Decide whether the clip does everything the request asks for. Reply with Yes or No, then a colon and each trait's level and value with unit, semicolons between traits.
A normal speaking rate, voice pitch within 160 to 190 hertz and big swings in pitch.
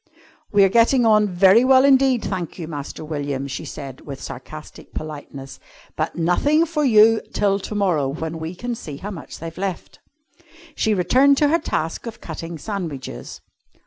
Yes: average, 165 wpm; medium, 185 Hz; wide, 6.8 semitones